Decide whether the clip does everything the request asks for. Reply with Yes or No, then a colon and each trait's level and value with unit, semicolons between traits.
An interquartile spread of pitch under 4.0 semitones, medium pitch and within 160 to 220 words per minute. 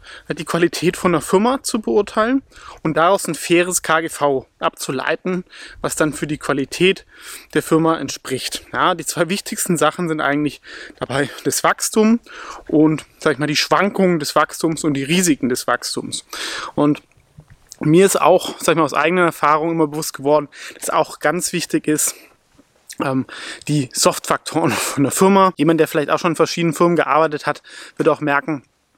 Yes: average, 3.2 semitones; medium, 160 Hz; average, 165 wpm